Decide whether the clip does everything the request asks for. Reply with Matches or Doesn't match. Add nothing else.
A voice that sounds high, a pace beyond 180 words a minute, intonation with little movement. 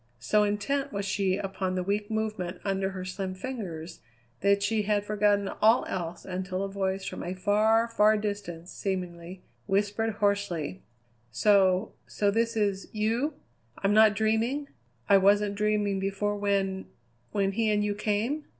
Doesn't match